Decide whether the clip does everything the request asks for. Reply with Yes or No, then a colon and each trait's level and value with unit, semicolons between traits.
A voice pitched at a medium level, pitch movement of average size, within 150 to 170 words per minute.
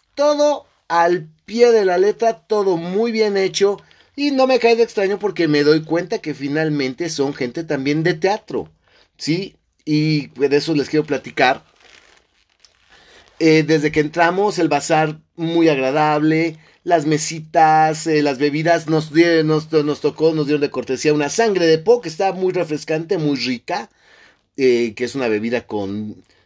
Yes: medium, 155 Hz; average, 3.7 semitones; average, 165 wpm